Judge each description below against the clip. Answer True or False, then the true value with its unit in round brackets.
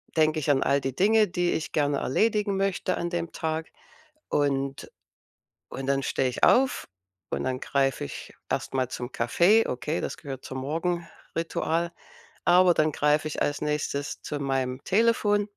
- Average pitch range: True (4.5 semitones)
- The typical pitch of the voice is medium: True (155 Hz)